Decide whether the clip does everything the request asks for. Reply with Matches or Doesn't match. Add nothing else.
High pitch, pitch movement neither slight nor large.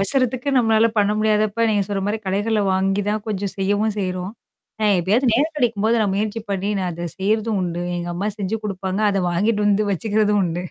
Doesn't match